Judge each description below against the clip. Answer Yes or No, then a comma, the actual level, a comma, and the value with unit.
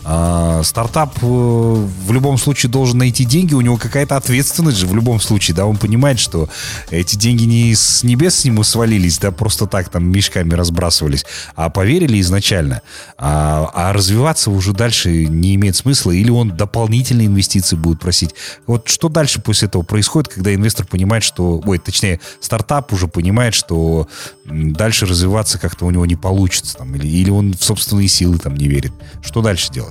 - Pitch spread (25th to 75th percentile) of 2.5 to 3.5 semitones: No, average, 5.0 semitones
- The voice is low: Yes, low, 100 Hz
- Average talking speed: No, fast, 175 wpm